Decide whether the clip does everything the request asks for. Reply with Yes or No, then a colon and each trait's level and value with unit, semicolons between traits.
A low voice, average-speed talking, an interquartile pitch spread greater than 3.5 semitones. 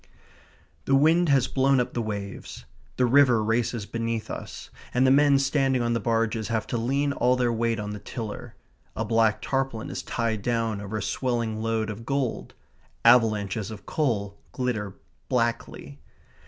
No: low, 115 Hz; average, 165 wpm; average, 3.0 semitones